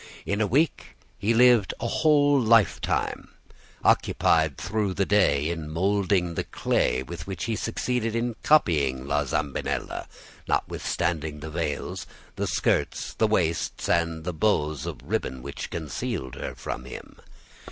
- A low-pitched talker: Yes, very low, 85 Hz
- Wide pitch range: Yes, wide, 6.6 semitones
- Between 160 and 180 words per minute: No, average, 140 wpm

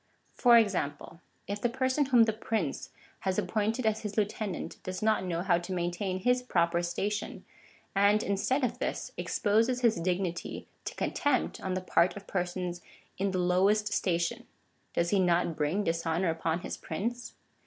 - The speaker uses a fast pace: No, average, 165 wpm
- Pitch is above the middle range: Yes, high, 195 Hz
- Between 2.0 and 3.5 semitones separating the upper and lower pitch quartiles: No, average, 4.0 semitones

